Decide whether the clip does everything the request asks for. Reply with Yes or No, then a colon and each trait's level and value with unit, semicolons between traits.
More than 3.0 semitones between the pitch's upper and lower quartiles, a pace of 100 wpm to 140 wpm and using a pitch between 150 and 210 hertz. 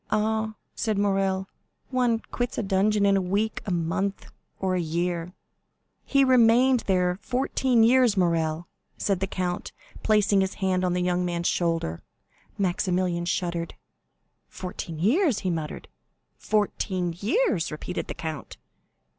Yes: average, 3.6 semitones; slow, 135 wpm; high, 190 Hz